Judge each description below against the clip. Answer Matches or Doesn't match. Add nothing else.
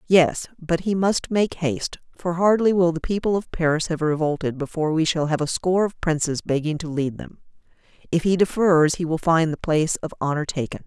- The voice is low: Doesn't match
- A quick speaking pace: Matches